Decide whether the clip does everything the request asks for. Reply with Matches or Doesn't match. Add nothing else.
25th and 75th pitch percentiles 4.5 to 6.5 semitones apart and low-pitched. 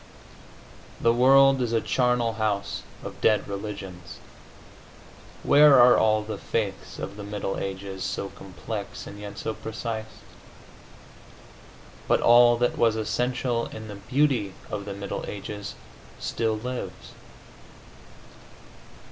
Doesn't match